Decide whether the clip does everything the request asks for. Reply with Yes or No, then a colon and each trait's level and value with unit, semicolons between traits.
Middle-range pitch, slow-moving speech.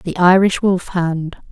Yes: medium, 180 Hz; slow, 120 wpm